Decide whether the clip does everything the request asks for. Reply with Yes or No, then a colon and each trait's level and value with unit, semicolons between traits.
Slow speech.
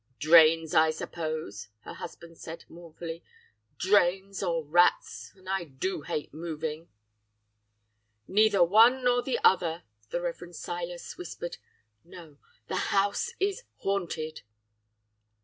Yes: slow, 115 wpm